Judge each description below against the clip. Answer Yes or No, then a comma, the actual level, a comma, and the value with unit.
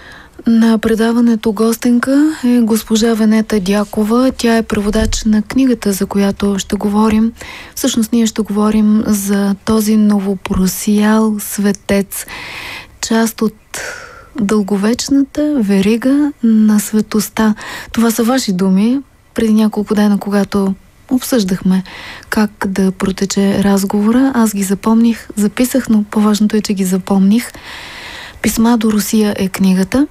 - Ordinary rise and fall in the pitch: No, narrow, 2.3 semitones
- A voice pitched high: Yes, high, 215 Hz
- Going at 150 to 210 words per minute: No, slow, 115 wpm